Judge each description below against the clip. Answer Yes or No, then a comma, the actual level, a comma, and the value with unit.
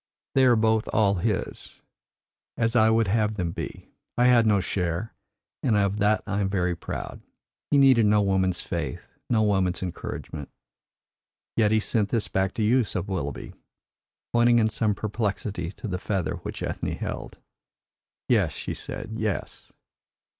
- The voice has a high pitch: No, low, 105 Hz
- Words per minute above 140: Yes, average, 155 wpm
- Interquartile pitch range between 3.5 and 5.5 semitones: No, average, 3.1 semitones